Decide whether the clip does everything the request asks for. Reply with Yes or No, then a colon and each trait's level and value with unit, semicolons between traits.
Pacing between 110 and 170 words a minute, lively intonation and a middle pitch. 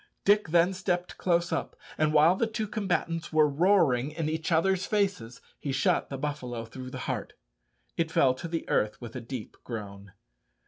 No: average, 180 wpm; wide, 5.8 semitones; medium, 155 Hz